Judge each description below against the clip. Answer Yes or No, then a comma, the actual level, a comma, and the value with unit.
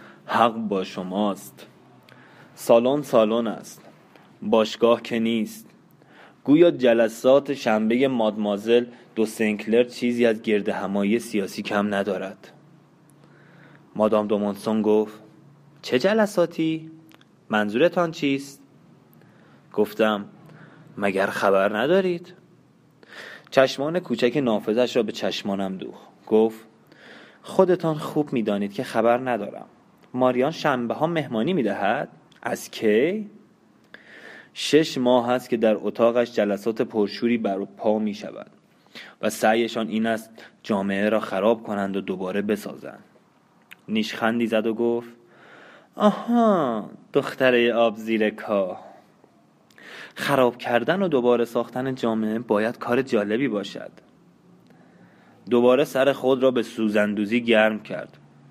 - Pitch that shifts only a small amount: No, average, 3.8 semitones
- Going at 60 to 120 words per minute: Yes, average, 110 wpm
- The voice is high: No, low, 115 Hz